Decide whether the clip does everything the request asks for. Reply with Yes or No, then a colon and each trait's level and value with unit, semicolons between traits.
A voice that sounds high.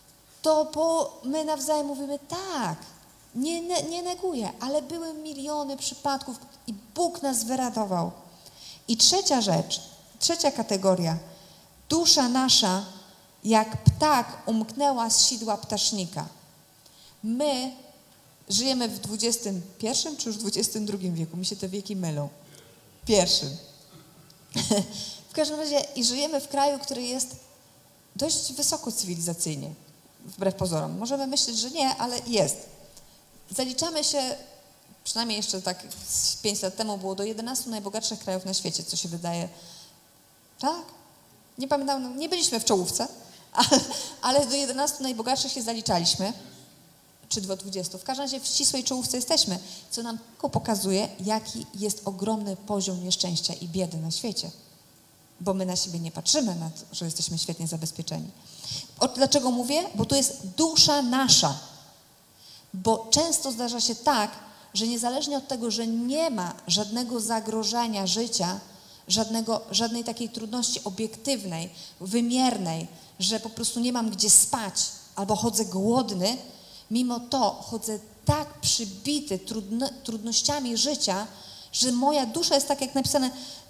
Yes: high, 225 Hz